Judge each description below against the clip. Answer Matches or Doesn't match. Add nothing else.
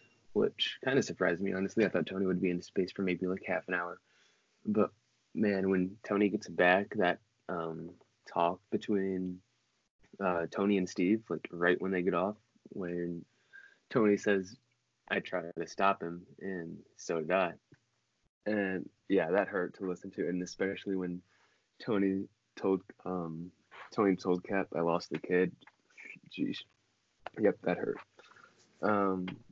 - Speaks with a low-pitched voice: Matches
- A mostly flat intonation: Matches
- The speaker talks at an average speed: Matches